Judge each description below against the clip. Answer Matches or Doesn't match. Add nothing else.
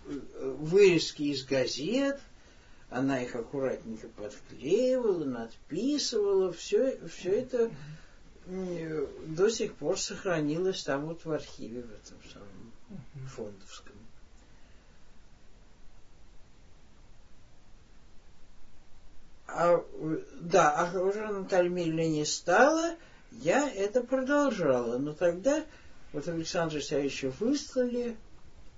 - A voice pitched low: Doesn't match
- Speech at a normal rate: Doesn't match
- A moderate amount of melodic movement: Doesn't match